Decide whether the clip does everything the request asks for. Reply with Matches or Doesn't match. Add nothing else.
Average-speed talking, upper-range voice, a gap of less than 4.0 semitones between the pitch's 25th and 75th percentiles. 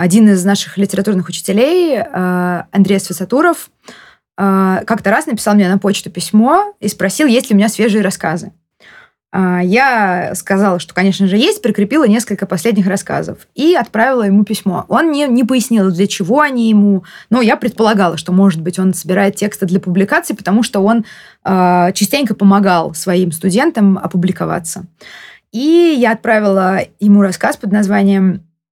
Matches